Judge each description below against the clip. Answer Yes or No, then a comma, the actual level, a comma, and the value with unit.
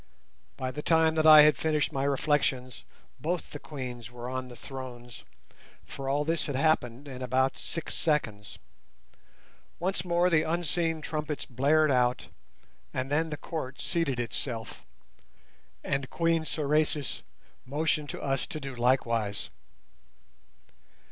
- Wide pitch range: No, average, 3.6 semitones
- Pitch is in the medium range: Yes, medium, 145 Hz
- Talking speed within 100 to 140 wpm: Yes, slow, 135 wpm